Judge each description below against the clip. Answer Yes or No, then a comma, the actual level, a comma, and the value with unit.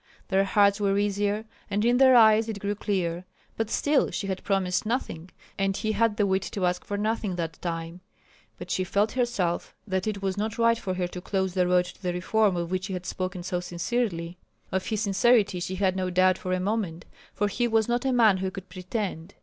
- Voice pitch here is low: No, high, 195 Hz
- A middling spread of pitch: Yes, average, 3.0 semitones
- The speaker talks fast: Yes, fast, 220 wpm